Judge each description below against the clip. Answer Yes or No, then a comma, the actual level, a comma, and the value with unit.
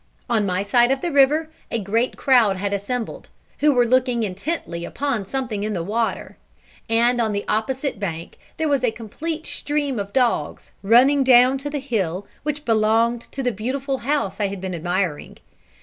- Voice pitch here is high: Yes, high, 235 Hz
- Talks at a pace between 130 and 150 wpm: No, average, 180 wpm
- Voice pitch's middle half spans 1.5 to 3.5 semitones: No, average, 5.0 semitones